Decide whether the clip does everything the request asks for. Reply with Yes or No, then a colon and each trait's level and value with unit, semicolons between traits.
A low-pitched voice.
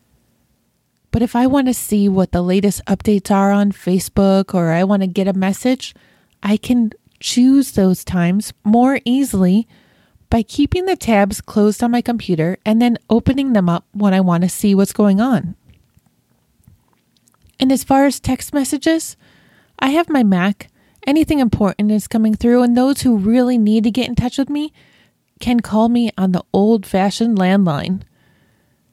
No: high, 215 Hz